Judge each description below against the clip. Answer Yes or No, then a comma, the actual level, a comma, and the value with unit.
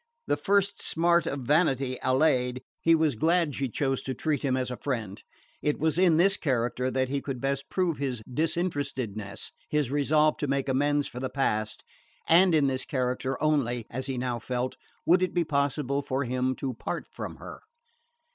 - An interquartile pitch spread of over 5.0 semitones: No, average, 3.4 semitones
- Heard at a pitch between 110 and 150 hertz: Yes, low, 135 Hz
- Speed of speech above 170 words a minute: Yes, average, 185 wpm